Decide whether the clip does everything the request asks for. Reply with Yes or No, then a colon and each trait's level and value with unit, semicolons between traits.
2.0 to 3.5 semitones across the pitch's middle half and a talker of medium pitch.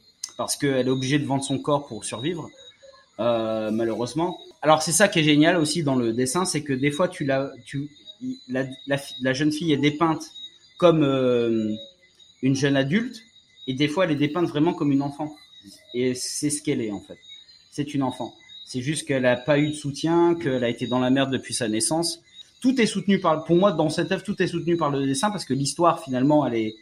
No: average, 4.6 semitones; medium, 145 Hz